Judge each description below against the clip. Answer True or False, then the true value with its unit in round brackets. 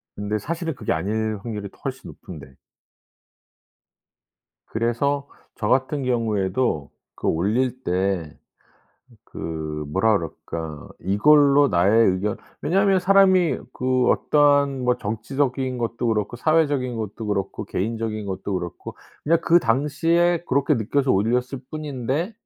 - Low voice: True (120 Hz)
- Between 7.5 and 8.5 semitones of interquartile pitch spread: False (5.8 semitones)